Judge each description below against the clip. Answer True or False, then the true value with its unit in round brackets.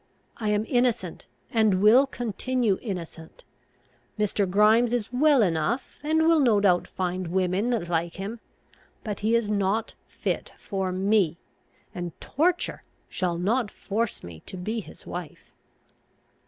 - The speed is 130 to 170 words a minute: True (140 wpm)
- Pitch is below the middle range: False (210 Hz)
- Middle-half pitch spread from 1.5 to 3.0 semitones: False (4.3 semitones)